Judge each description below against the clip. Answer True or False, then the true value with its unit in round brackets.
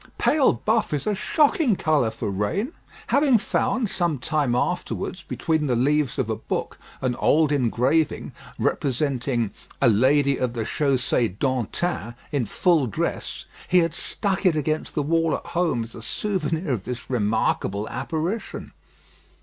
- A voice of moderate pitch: True (145 Hz)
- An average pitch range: False (5.9 semitones)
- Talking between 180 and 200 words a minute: False (150 wpm)